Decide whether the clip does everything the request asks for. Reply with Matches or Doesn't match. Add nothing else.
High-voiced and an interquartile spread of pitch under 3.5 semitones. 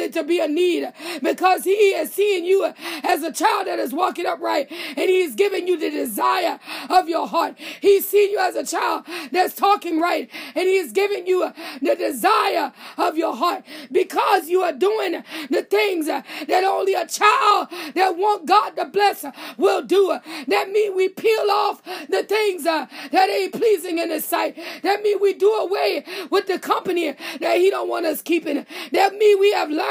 Matches